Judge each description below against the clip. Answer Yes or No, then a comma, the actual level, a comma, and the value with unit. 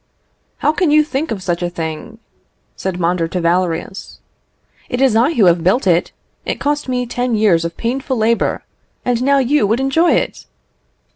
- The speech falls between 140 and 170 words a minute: No, average, 185 wpm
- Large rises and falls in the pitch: Yes, wide, 7.2 semitones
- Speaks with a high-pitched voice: Yes, high, 225 Hz